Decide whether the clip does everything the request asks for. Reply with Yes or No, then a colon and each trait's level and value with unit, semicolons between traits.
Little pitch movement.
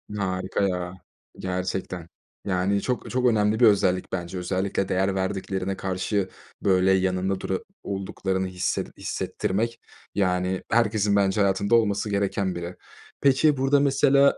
Yes: narrow, 2.1 semitones